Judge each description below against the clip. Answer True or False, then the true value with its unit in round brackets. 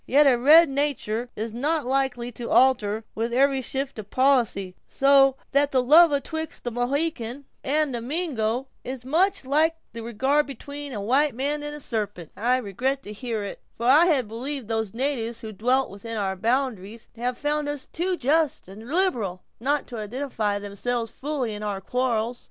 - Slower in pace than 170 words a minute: False (180 wpm)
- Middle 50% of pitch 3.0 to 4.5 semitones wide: True (4.2 semitones)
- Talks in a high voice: True (255 Hz)